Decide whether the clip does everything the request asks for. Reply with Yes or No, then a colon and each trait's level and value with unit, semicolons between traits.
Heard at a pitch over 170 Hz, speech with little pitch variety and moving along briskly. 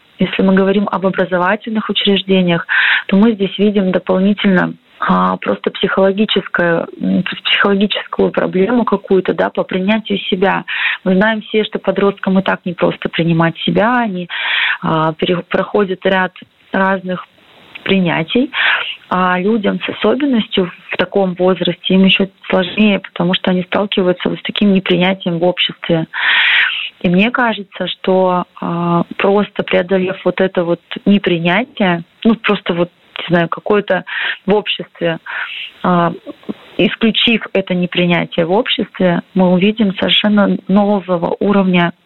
No: high, 190 Hz; narrow, 2.3 semitones; average, 125 wpm